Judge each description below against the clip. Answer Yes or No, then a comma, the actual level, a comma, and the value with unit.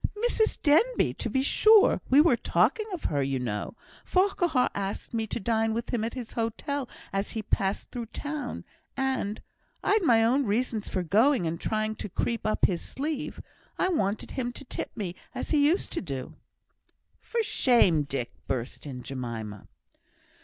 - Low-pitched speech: No, high, 230 Hz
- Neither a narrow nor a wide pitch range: No, wide, 7.3 semitones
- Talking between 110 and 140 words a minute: No, average, 170 wpm